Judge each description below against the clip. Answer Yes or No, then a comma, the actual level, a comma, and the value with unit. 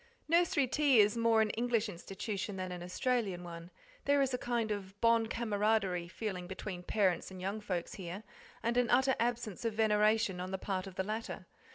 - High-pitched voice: Yes, high, 210 Hz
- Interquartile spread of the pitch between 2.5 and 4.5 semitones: Yes, average, 3.7 semitones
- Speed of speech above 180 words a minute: Yes, average, 190 wpm